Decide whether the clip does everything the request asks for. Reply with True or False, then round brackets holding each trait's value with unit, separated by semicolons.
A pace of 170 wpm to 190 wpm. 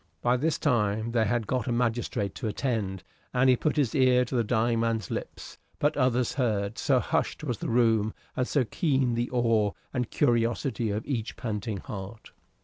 True (185 wpm)